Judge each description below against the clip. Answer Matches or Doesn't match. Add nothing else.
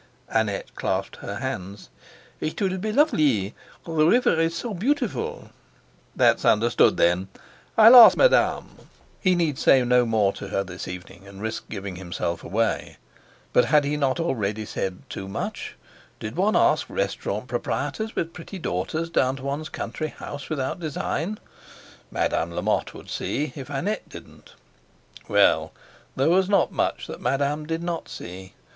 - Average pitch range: Doesn't match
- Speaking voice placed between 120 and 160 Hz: Matches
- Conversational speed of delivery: Matches